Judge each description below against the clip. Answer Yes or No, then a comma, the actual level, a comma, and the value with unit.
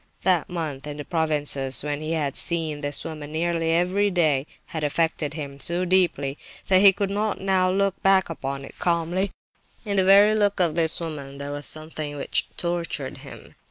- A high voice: No, medium, 165 Hz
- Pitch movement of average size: Yes, average, 4.0 semitones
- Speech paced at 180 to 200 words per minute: Yes, average, 185 wpm